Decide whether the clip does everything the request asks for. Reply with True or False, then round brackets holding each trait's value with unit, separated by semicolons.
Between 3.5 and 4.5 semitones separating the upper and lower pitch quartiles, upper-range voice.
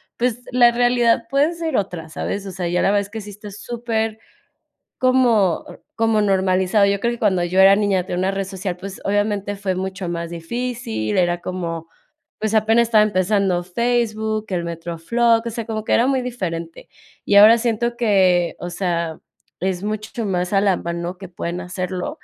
True (4.0 semitones; 200 Hz)